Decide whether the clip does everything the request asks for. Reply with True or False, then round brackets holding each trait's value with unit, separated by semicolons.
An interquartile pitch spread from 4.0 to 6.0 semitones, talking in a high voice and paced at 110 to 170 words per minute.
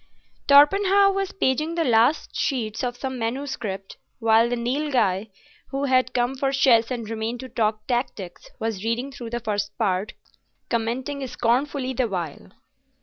False (3.4 semitones; 245 Hz; 145 wpm)